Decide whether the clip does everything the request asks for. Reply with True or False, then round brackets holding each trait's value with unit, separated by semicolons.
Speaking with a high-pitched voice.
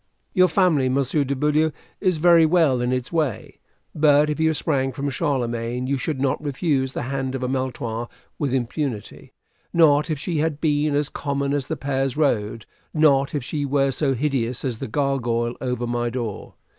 False (140 Hz)